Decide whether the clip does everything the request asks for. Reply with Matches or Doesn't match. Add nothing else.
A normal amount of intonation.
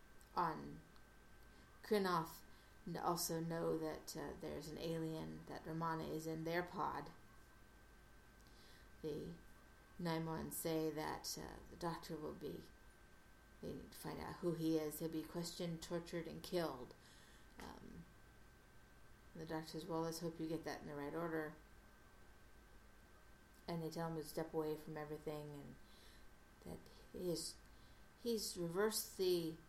Doesn't match